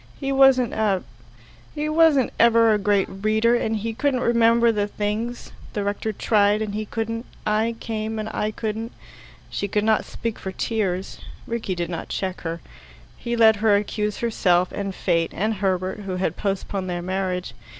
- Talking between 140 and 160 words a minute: No, average, 175 wpm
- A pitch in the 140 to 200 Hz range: No, high, 215 Hz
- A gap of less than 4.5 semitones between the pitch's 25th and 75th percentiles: Yes, average, 2.9 semitones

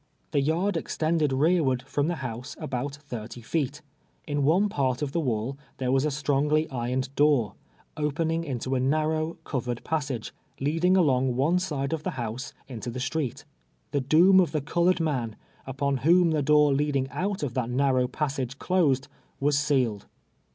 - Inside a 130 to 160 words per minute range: No, average, 170 wpm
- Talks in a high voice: No, medium, 140 Hz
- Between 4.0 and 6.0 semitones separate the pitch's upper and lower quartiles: No, average, 3.4 semitones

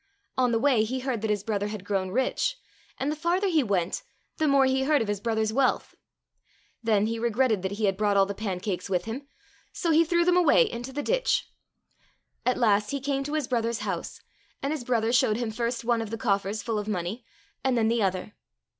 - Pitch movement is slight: No, average, 4.5 semitones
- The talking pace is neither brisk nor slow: No, fast, 220 wpm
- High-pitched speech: Yes, high, 230 Hz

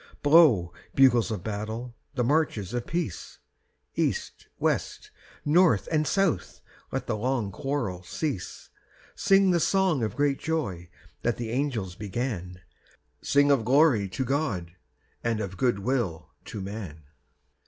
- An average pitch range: No, wide, 6.4 semitones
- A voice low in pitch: Yes, low, 120 Hz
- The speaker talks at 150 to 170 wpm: No, slow, 135 wpm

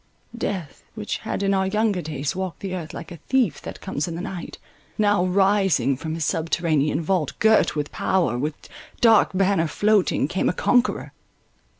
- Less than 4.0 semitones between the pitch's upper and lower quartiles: No, average, 4.3 semitones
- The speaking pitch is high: No, medium, 180 Hz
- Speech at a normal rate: Yes, average, 175 wpm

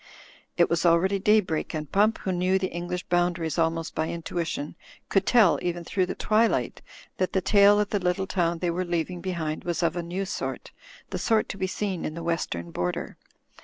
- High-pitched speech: No, medium, 175 Hz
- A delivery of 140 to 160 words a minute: No, average, 200 wpm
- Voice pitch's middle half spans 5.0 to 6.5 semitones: No, narrow, 2.4 semitones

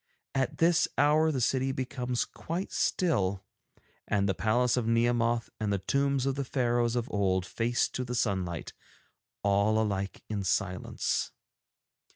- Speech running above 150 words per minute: No, average, 145 wpm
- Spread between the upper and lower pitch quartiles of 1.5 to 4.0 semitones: No, average, 4.6 semitones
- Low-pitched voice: Yes, low, 120 Hz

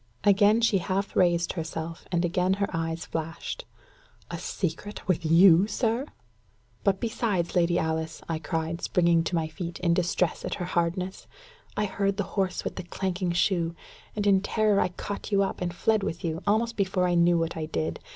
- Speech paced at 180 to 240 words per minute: Yes, average, 185 wpm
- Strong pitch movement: No, average, 2.9 semitones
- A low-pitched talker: No, medium, 180 Hz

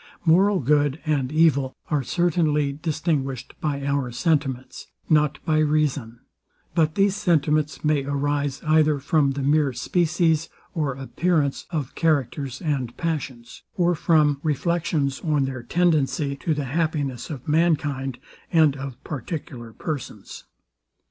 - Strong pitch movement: No, average, 2.7 semitones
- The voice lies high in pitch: No, medium, 150 Hz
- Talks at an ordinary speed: No, slow, 125 wpm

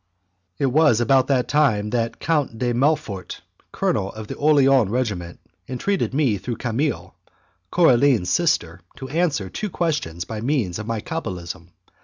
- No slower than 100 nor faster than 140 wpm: No, average, 150 wpm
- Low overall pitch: Yes, low, 125 Hz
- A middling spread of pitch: No, wide, 5.7 semitones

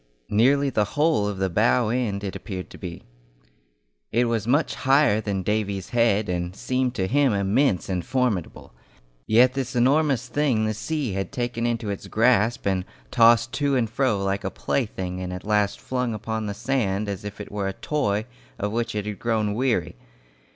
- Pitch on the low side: Yes, low, 110 Hz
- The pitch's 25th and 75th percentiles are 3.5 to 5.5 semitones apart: Yes, average, 4.0 semitones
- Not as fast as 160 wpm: No, average, 185 wpm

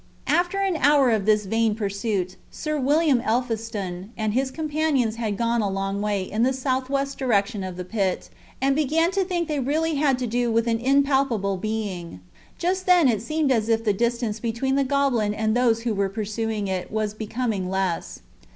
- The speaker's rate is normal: Yes, average, 190 wpm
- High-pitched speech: Yes, high, 230 Hz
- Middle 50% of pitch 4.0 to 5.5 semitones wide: Yes, average, 4.7 semitones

